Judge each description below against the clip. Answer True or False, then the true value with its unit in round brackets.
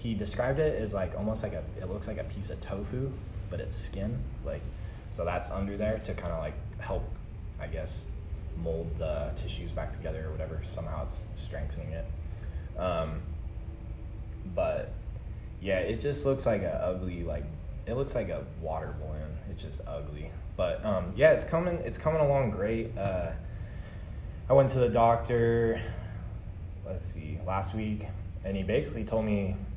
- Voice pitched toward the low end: True (95 Hz)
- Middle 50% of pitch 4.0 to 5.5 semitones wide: True (4.6 semitones)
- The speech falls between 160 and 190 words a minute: True (170 wpm)